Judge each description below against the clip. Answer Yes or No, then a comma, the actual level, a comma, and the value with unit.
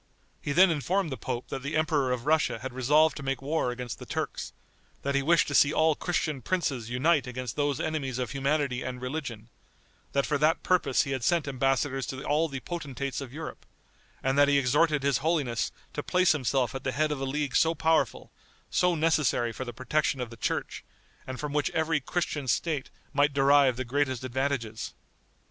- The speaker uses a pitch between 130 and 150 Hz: Yes, medium, 140 Hz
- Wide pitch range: No, average, 3.0 semitones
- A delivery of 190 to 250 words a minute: Yes, average, 200 wpm